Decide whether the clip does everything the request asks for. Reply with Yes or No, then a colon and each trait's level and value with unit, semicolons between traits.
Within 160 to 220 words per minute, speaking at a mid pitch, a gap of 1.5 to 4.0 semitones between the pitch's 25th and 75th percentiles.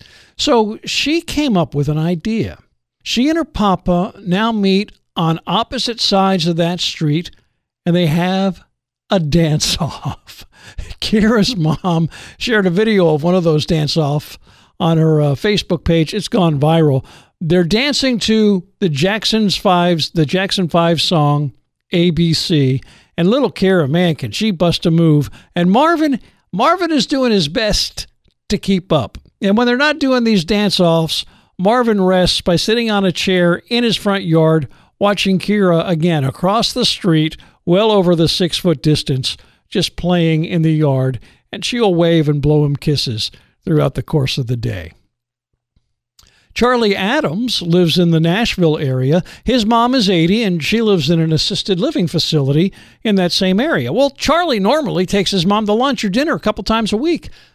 No: average, 170 wpm; medium, 180 Hz; average, 4.8 semitones